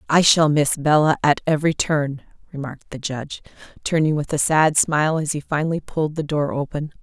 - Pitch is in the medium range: Yes, medium, 150 Hz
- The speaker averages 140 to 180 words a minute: No, average, 190 wpm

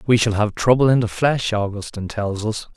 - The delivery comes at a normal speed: No, fast, 215 wpm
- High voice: No, low, 110 Hz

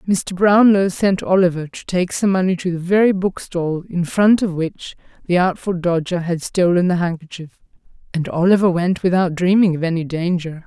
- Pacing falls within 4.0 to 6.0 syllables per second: Yes, 5.0 syllables/s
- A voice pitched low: No, medium, 180 Hz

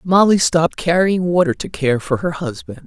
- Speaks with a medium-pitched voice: Yes, medium, 175 Hz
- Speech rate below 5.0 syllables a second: No, 5.1 syllables/s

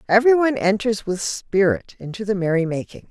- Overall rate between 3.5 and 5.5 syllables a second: No, 5.9 syllables/s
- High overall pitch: Yes, high, 205 Hz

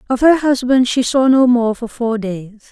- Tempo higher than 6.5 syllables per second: No, 4.5 syllables/s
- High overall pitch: Yes, high, 245 Hz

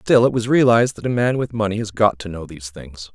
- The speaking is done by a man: Yes, male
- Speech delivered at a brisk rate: Yes, fast, 285 wpm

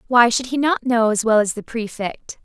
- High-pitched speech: Yes, high, 235 Hz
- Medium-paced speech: No, fast, 245 wpm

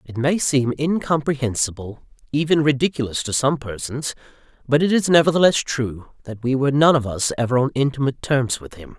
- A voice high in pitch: No, low, 135 Hz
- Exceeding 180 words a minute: No, average, 175 wpm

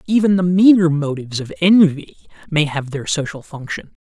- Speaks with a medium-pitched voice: Yes, medium, 160 Hz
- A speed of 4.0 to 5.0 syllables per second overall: No, 5.3 syllables/s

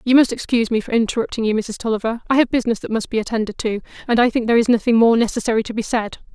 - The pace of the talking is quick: Yes, fast, 265 wpm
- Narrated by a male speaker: No, female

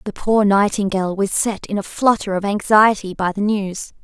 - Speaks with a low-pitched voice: No, high, 200 Hz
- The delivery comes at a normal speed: No, fast, 210 wpm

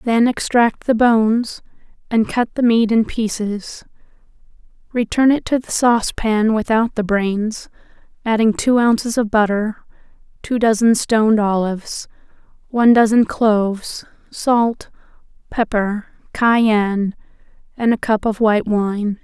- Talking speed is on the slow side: Yes, slow, 120 wpm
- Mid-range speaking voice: No, high, 220 Hz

